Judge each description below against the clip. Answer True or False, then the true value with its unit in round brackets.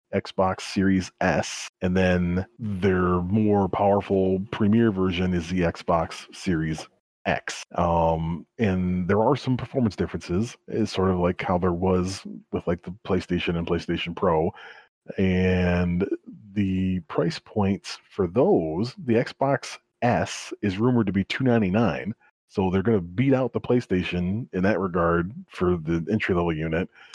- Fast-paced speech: False (145 wpm)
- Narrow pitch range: False (3.1 semitones)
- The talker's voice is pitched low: True (95 Hz)